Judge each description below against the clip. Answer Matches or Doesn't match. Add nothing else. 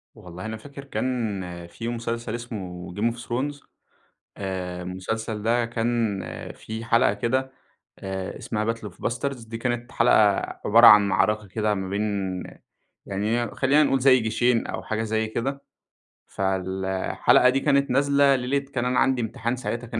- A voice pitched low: Matches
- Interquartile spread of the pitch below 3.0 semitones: Doesn't match